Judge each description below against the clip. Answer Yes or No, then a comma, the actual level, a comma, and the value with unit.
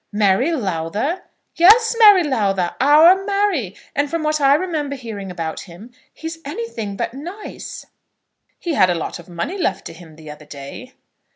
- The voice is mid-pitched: No, very high, 255 Hz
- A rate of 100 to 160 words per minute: No, average, 170 wpm